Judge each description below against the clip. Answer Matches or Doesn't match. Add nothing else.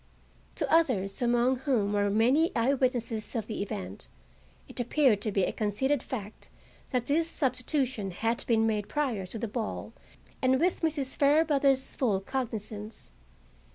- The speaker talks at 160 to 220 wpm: Doesn't match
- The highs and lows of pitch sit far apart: Doesn't match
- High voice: Matches